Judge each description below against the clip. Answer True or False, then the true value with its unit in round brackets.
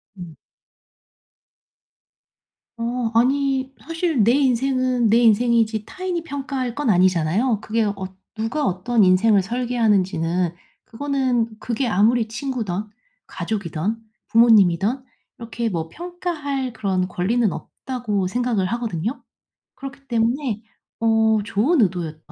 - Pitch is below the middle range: False (230 Hz)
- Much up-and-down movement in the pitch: False (4.4 semitones)